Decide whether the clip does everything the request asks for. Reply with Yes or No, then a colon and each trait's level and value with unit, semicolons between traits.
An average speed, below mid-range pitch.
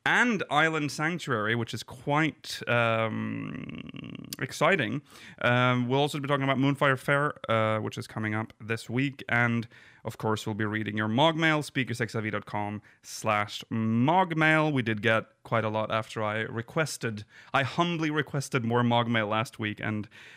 Yes: average, 150 wpm; low, 120 Hz